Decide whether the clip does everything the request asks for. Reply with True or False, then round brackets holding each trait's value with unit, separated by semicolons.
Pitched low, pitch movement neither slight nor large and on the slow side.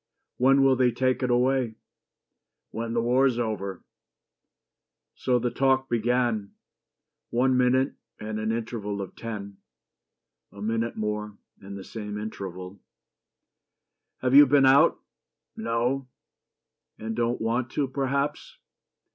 True (120 Hz; 3.2 semitones; 120 wpm)